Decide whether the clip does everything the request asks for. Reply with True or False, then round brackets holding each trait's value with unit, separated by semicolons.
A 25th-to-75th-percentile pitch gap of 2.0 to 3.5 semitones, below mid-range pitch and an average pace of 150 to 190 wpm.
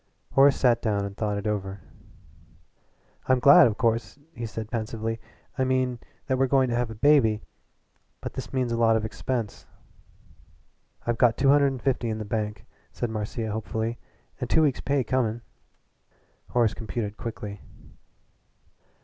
True (3.0 semitones; 115 Hz; 160 wpm)